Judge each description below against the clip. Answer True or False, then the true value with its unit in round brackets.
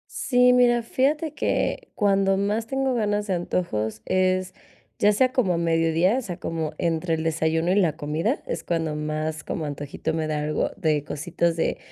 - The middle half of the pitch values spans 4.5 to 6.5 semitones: True (4.9 semitones)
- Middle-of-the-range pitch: True (175 Hz)